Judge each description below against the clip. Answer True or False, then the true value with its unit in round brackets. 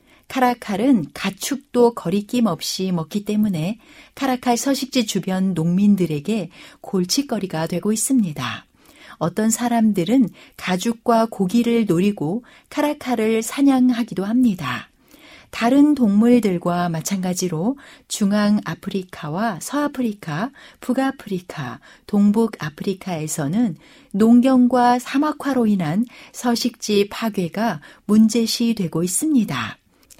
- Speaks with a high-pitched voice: True (220 Hz)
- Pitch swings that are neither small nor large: True (4.8 semitones)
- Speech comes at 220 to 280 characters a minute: True (255 characters per minute)